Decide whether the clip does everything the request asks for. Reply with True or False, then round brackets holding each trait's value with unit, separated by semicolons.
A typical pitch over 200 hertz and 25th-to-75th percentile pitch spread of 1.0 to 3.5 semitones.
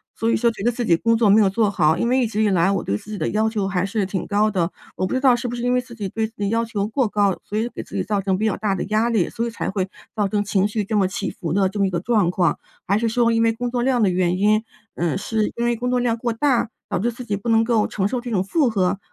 True (215 Hz; 3.1 semitones)